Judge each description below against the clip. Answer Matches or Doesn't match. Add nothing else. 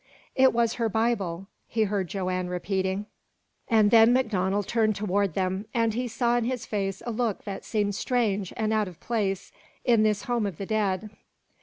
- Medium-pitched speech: Doesn't match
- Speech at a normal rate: Matches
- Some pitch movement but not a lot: Matches